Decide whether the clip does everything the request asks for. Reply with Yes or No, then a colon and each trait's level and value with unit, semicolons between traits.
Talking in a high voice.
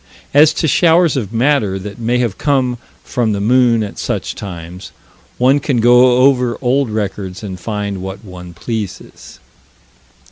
No: low, 115 Hz